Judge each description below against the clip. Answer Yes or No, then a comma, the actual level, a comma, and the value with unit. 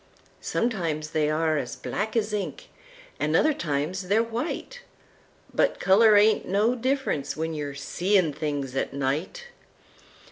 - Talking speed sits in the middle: No, slow, 130 wpm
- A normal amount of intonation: No, wide, 7.0 semitones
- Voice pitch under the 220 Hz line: Yes, medium, 185 Hz